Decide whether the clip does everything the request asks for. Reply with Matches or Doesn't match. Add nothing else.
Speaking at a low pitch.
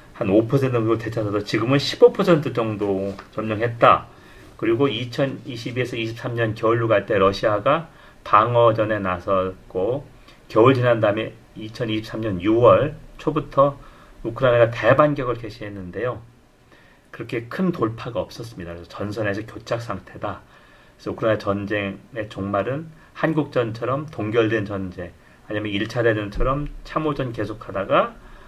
Matches